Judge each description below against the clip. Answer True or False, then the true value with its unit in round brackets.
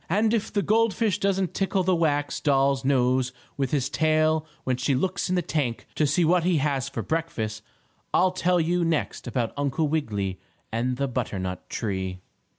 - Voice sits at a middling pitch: True (145 Hz)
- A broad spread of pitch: True (5.9 semitones)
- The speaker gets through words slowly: False (180 wpm)